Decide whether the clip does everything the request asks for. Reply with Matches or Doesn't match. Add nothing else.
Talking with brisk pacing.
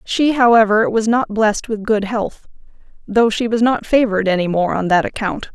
Doesn't match